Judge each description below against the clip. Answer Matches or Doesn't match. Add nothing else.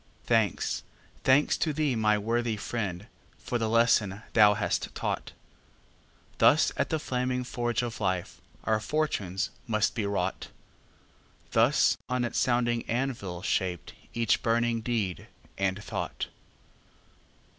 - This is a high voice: Doesn't match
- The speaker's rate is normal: Doesn't match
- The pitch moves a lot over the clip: Doesn't match